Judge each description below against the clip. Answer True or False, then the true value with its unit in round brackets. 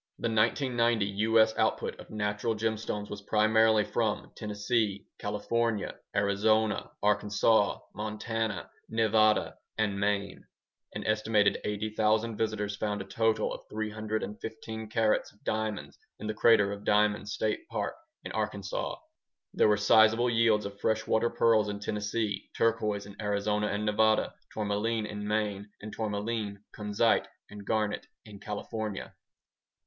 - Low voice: True (105 Hz)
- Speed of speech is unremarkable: False (125 wpm)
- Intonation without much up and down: True (1.2 semitones)